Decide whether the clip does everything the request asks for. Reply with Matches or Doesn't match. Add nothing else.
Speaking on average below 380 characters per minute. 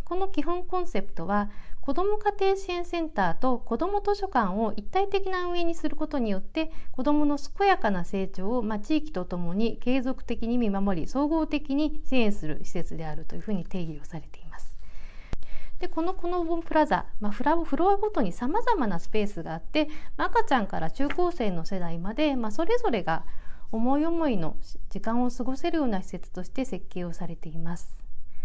Doesn't match